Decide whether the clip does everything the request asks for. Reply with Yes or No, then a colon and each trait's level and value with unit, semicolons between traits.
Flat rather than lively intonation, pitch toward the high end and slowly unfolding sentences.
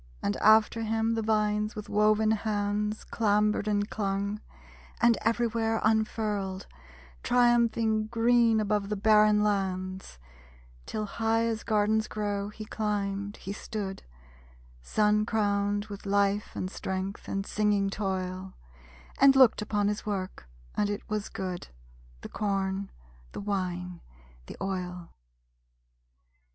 Yes: narrow, 1.7 semitones; high, 210 Hz; slow, 120 wpm